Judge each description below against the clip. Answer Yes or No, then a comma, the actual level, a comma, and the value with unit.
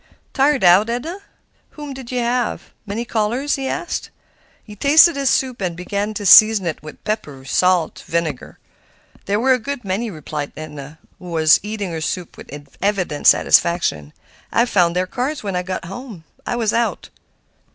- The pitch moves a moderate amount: No, wide, 6.3 semitones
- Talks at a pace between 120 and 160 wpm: No, average, 180 wpm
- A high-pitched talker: Yes, high, 205 Hz